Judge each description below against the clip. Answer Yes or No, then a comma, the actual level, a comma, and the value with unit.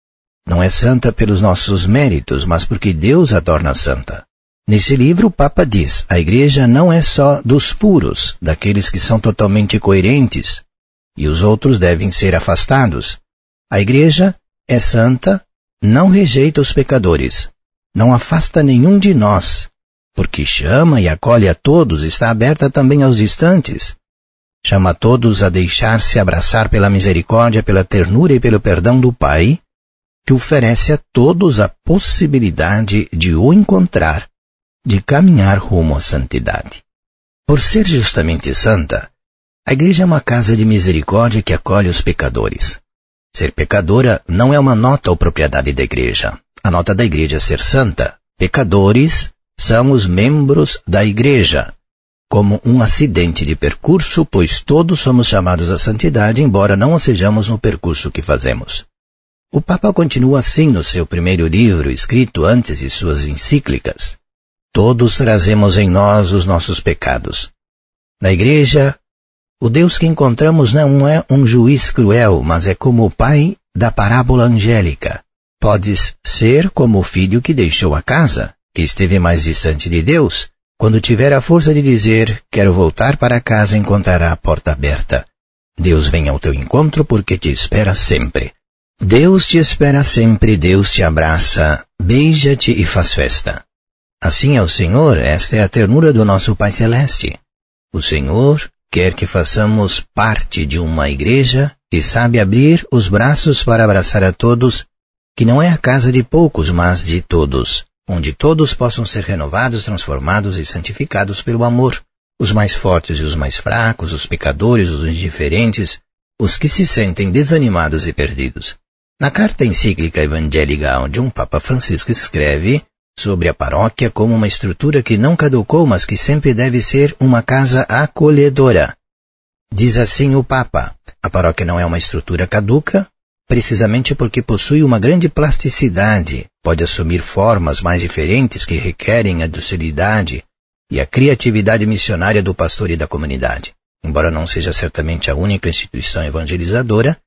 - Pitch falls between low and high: No, low, 105 Hz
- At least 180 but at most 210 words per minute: No, average, 150 wpm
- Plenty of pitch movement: Yes, wide, 7.1 semitones